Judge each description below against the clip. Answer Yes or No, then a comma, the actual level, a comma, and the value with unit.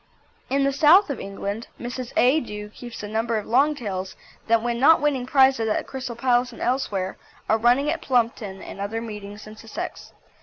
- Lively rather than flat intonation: No, average, 3.8 semitones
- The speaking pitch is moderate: No, high, 235 Hz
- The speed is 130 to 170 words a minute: No, average, 190 wpm